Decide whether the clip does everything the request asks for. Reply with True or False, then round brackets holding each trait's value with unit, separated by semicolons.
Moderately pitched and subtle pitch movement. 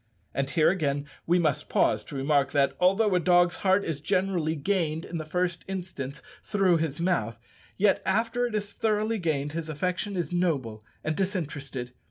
False (170 Hz; 4.6 semitones)